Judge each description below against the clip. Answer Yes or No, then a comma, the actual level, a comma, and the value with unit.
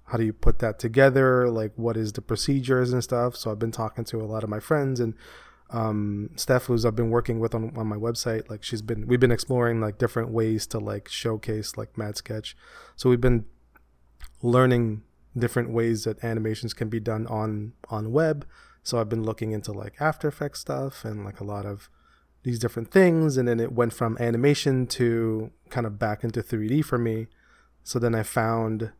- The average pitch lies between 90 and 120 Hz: Yes, low, 115 Hz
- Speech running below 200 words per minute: No, fast, 205 wpm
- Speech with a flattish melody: Yes, narrow, 2.1 semitones